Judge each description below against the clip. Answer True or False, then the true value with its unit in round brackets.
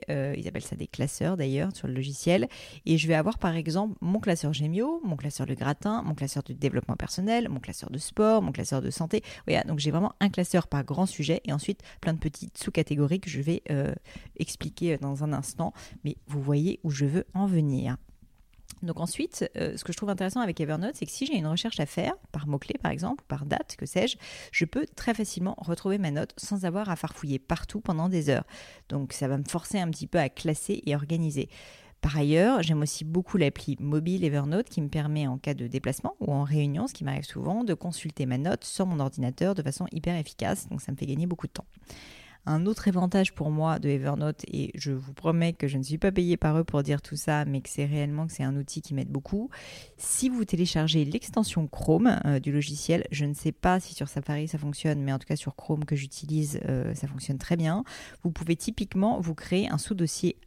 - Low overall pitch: False (155 Hz)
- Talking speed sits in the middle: False (230 wpm)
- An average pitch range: True (4.1 semitones)